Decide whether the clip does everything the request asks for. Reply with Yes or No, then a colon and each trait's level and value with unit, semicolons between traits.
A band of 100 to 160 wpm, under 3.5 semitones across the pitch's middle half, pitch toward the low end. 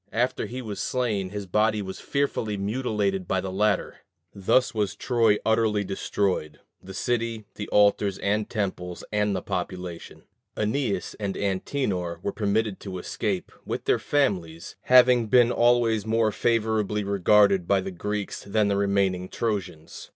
Yes: average, 145 wpm; average, 2.7 semitones; low, 105 Hz